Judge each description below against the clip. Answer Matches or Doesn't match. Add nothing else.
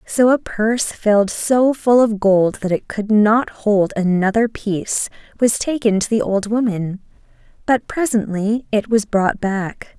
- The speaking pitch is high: Matches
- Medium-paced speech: Matches